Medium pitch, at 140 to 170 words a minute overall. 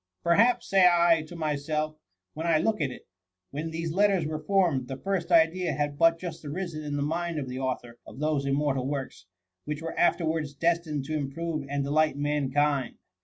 No: medium, 155 Hz; fast, 205 wpm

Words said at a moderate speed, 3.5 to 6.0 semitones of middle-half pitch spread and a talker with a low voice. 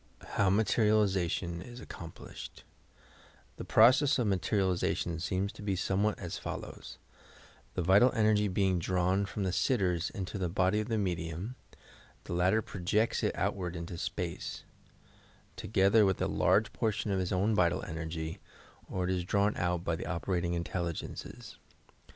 No: average, 150 wpm; average, 3.1 semitones; very low, 95 Hz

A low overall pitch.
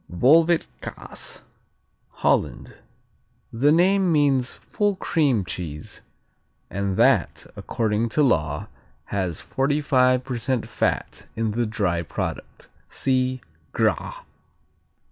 Yes: low, 125 Hz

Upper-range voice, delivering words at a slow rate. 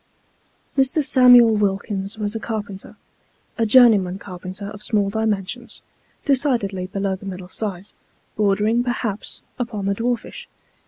Yes: high, 210 Hz; slow, 120 wpm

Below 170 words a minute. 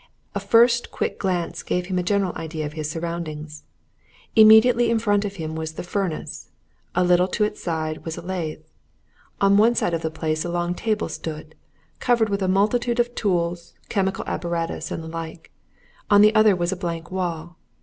No: average, 190 wpm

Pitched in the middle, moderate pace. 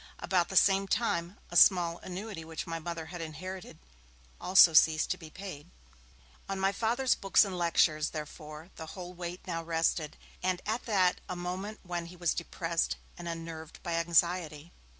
Yes: medium, 175 Hz; average, 170 wpm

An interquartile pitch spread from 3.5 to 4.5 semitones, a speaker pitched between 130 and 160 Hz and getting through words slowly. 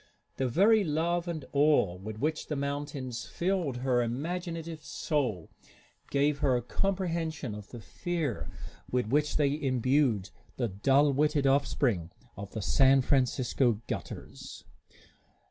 Yes: average, 4.2 semitones; medium, 140 Hz; slow, 120 wpm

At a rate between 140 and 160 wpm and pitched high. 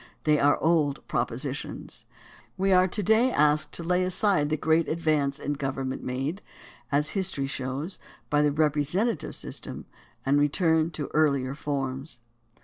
No: average, 145 wpm; medium, 150 Hz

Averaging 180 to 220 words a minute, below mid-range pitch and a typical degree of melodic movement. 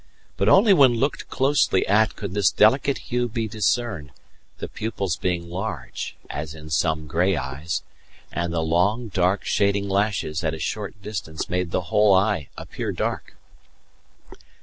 No: average, 150 wpm; very low, 95 Hz; average, 4.7 semitones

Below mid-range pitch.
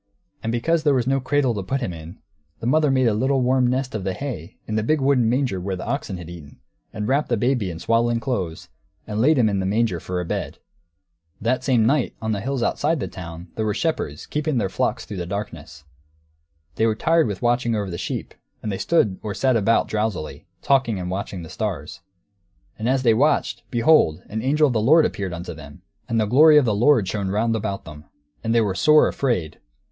Yes: low, 115 Hz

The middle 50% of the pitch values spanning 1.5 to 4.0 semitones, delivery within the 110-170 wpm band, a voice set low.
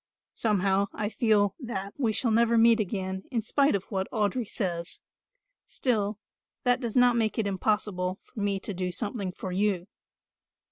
No: average, 3.2 semitones; average, 160 wpm; high, 210 Hz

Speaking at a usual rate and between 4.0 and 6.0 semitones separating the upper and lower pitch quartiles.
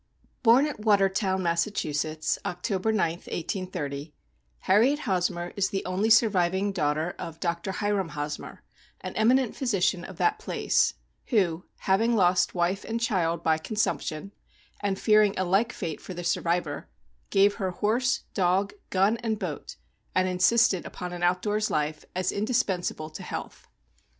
No: average, 155 wpm; average, 3.6 semitones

